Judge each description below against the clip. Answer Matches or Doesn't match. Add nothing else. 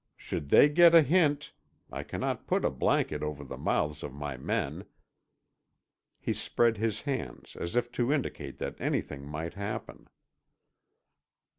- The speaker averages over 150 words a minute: Doesn't match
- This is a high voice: Doesn't match